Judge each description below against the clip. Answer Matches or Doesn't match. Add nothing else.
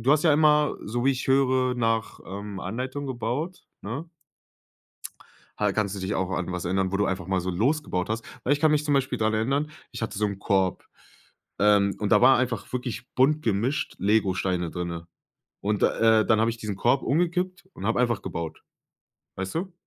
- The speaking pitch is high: Doesn't match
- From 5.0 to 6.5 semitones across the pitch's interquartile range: Matches